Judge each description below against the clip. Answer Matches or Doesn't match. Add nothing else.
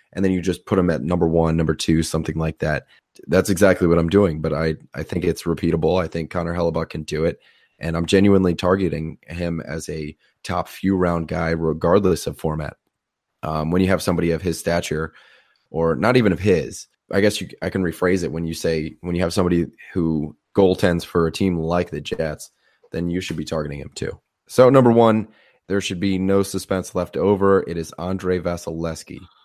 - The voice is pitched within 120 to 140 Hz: Doesn't match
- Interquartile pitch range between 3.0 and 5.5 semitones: Doesn't match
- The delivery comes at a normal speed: Doesn't match